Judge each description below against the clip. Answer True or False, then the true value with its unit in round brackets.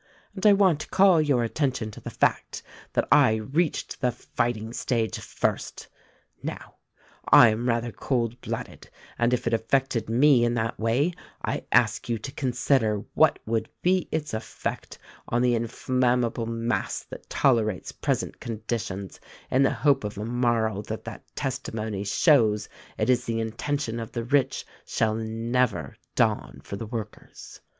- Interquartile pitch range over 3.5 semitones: False (2.9 semitones)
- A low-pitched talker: True (120 Hz)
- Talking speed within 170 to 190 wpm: False (155 wpm)